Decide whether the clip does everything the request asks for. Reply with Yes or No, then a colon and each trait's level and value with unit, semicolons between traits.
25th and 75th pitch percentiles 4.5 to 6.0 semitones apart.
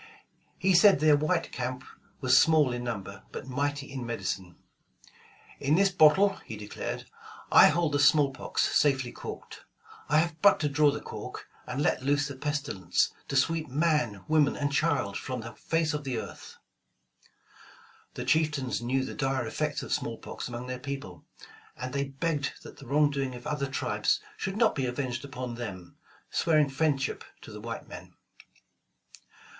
No: average, 3.1 semitones